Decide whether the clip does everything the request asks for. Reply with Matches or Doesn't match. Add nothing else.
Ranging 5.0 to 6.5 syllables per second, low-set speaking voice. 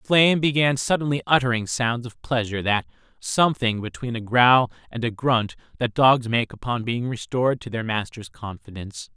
Matches